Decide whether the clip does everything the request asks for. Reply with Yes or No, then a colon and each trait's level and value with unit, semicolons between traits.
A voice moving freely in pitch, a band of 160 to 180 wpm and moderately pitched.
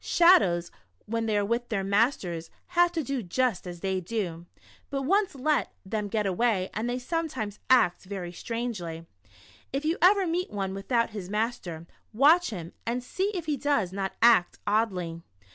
No: wide, 6.4 semitones; average, 170 wpm; high, 220 Hz